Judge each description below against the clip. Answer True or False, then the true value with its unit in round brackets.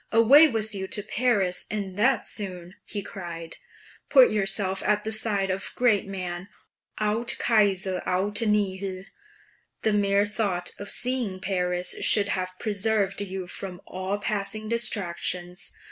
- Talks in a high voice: True (200 Hz)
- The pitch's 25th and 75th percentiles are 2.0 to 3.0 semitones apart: True (2.5 semitones)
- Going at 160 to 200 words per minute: False (135 wpm)